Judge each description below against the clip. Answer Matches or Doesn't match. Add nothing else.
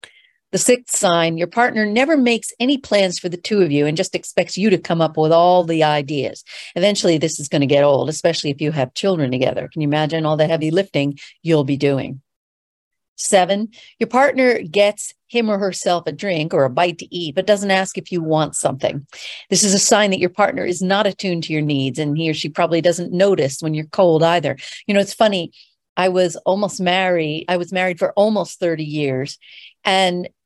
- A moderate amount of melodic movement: Matches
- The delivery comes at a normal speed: Doesn't match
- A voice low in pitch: Doesn't match